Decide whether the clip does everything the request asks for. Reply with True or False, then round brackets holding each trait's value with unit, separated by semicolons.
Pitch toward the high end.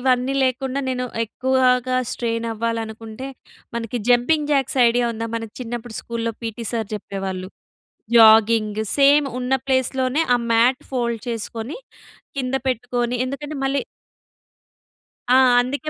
True (245 Hz)